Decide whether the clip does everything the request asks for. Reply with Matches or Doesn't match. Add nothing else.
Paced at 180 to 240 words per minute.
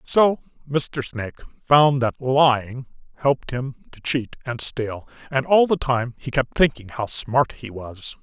Doesn't match